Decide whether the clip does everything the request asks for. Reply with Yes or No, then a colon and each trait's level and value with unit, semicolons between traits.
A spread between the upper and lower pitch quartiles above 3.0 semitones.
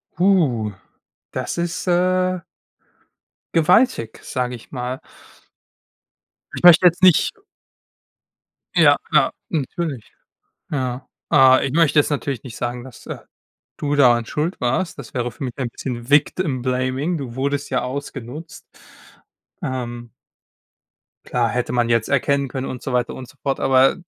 Yes: average, 3.8 semitones